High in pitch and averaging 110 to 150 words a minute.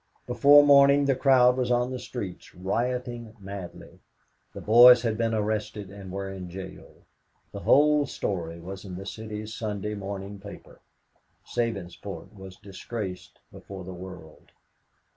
No: low, 105 Hz; average, 140 wpm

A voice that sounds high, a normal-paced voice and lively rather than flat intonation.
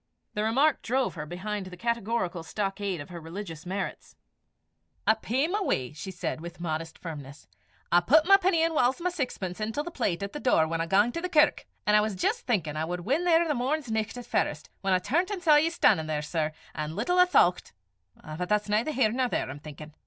No: high, 210 Hz; fast, 225 wpm; wide, 8.6 semitones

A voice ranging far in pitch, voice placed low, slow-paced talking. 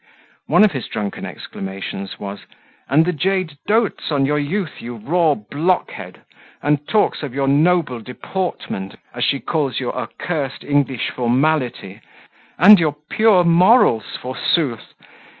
No: wide, 6.2 semitones; medium, 145 Hz; slow, 130 wpm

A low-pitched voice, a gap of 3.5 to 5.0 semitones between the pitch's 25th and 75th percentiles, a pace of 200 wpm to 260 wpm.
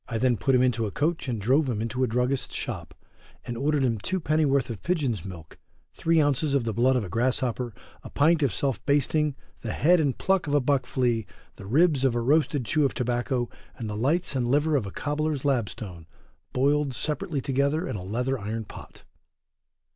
Yes: low, 130 Hz; average, 3.9 semitones; fast, 205 wpm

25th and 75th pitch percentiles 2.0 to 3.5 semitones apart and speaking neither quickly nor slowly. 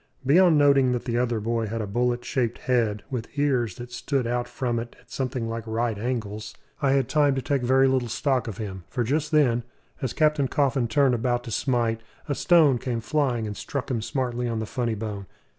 No: average, 2.9 semitones; fast, 210 wpm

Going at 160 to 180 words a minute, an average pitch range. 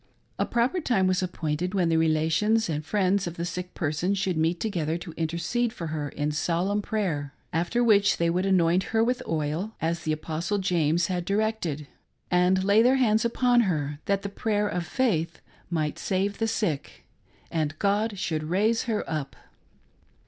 Yes: average, 175 wpm; average, 4.4 semitones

